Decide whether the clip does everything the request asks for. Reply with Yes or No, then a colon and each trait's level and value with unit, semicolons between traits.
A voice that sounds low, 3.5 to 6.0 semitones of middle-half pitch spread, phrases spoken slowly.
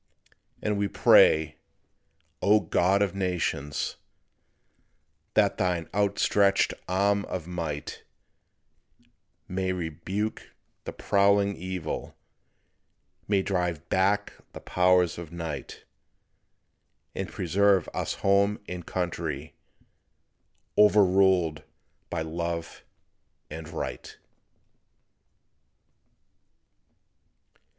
No: very low, 90 Hz; average, 3.1 semitones; slow, 80 wpm